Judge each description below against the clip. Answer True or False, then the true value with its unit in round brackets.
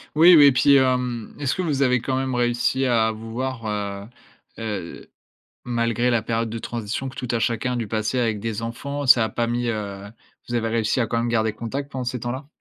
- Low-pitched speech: True (120 Hz)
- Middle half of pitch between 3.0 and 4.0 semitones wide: False (2.5 semitones)